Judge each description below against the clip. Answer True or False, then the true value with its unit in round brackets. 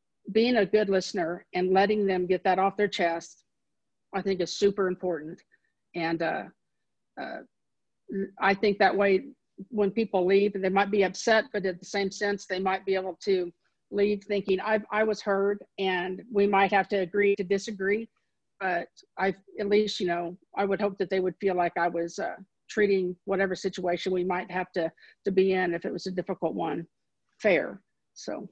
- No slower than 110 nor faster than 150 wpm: False (190 wpm)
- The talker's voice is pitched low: False (195 Hz)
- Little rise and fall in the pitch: True (1.8 semitones)